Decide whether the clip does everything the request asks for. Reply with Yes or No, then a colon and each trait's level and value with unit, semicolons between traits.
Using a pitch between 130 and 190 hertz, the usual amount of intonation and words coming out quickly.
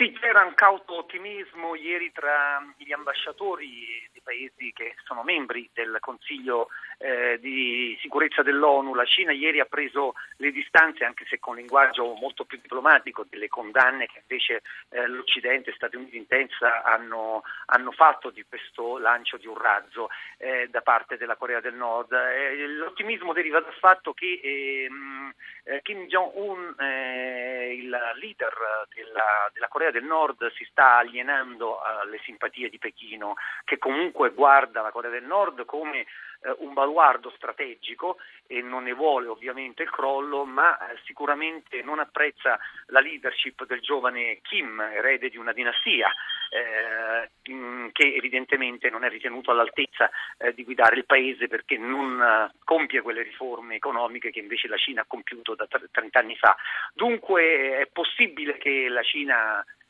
No: low, 135 Hz; average, 4.7 semitones; average, 150 wpm